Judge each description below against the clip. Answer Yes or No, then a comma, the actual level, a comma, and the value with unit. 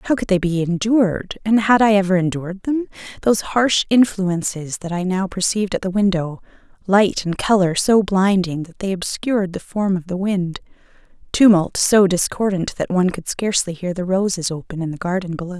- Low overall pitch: No, high, 190 Hz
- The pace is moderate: Yes, average, 180 wpm